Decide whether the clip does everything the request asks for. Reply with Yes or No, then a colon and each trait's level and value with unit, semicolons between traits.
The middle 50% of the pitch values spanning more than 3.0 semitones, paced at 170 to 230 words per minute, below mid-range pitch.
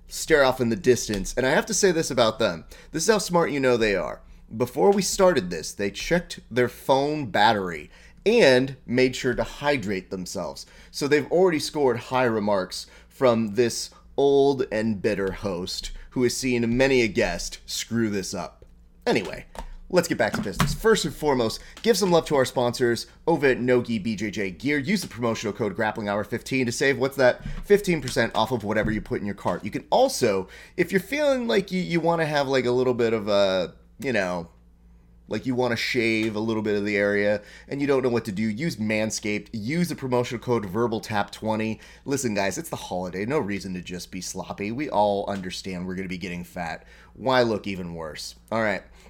Yes: wide, 5.5 semitones; fast, 205 wpm; low, 120 Hz